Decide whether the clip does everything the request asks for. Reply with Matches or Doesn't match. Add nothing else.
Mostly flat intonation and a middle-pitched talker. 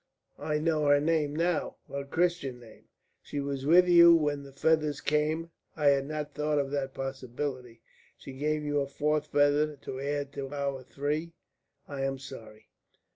Matches